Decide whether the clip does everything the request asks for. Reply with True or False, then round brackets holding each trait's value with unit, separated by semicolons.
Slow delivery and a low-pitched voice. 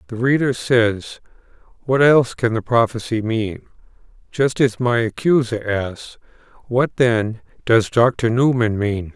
True (130 wpm; 120 Hz)